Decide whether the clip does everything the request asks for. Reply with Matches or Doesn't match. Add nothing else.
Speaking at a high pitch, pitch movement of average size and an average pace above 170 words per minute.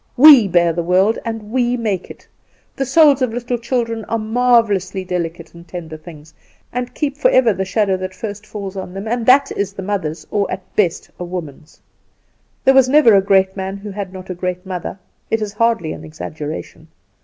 Matches